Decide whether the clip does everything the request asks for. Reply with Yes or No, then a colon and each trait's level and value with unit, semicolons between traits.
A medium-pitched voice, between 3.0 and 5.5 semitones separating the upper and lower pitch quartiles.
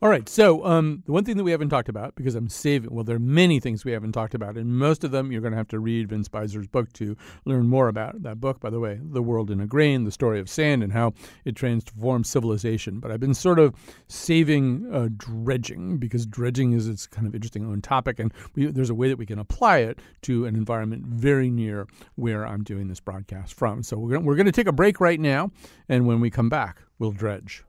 No: low, 120 Hz; average, 3.8 semitones